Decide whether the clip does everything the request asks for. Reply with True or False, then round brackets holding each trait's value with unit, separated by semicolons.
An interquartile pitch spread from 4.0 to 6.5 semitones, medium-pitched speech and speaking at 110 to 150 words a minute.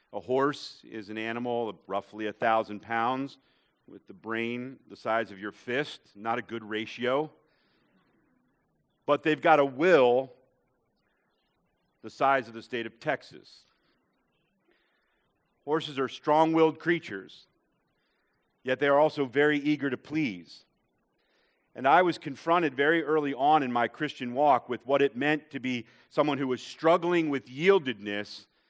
False (4.7 semitones; 130 Hz; 145 wpm)